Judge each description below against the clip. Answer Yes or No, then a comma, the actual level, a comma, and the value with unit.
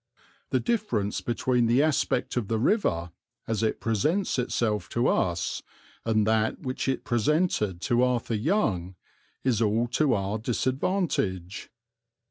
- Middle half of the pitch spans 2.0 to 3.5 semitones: No, average, 3.9 semitones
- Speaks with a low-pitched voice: Yes, low, 115 Hz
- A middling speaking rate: No, slow, 130 wpm